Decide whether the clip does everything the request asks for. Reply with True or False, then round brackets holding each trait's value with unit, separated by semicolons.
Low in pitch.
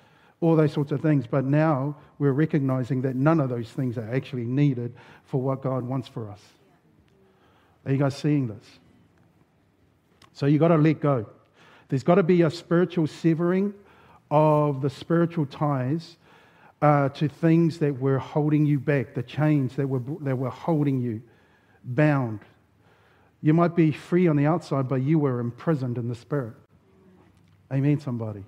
False (145 Hz)